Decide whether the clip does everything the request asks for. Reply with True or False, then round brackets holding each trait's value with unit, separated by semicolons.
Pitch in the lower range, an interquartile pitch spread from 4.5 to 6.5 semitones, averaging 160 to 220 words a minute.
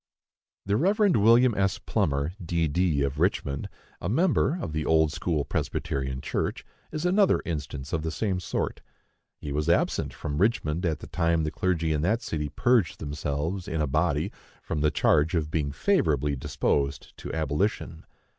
True (80 Hz; 4.8 semitones; 165 wpm)